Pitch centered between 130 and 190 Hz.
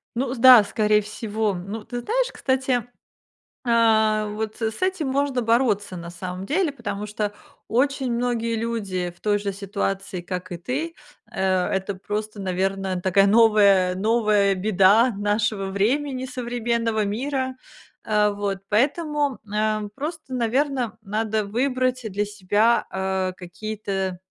No: high, 215 Hz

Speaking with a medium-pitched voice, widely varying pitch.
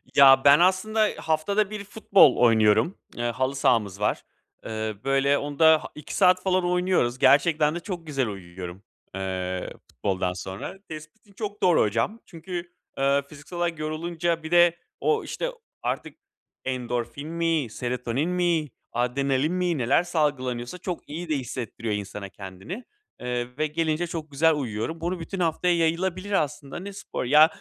Yes: medium, 150 Hz; wide, 6.0 semitones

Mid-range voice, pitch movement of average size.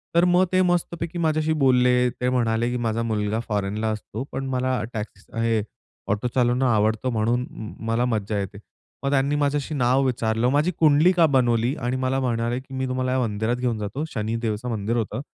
No: low, 125 Hz; average, 3.1 semitones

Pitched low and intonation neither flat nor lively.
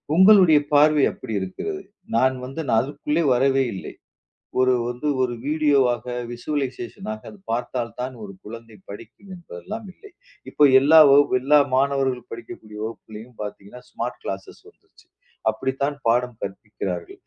Yes: low, 130 Hz; average, 4.3 semitones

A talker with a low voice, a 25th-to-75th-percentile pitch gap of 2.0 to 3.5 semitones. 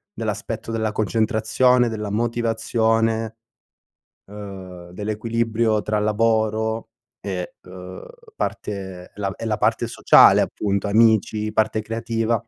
No: low, 110 Hz; narrow, 1.6 semitones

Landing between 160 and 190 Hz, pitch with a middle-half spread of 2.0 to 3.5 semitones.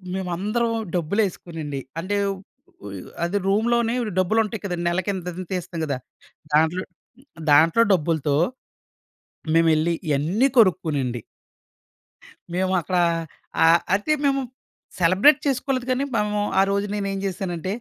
No: medium, 185 Hz; average, 4.0 semitones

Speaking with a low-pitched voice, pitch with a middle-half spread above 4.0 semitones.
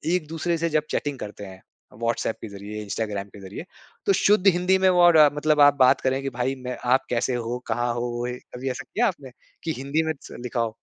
Yes: low, 130 Hz; wide, 5.5 semitones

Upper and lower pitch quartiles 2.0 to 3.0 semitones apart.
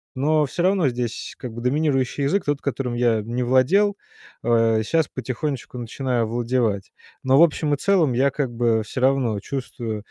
No: average, 3.6 semitones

